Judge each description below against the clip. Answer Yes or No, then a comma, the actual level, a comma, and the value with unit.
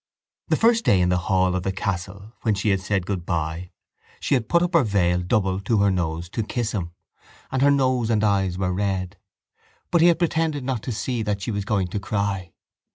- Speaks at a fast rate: Yes, fast, 220 wpm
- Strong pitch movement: No, average, 4.4 semitones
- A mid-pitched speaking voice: No, low, 100 Hz